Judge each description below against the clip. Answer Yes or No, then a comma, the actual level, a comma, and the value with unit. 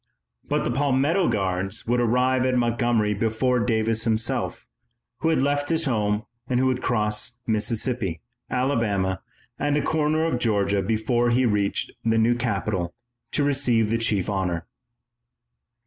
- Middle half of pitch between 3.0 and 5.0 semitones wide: Yes, average, 3.4 semitones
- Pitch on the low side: Yes, low, 115 Hz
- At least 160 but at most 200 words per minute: No, average, 145 wpm